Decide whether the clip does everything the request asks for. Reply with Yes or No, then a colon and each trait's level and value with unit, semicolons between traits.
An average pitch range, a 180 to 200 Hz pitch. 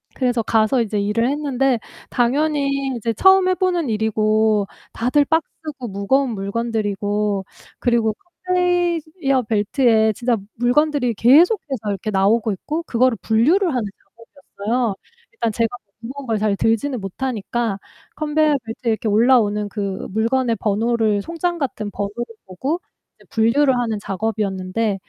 No: average, 4.6 semitones; high, 235 Hz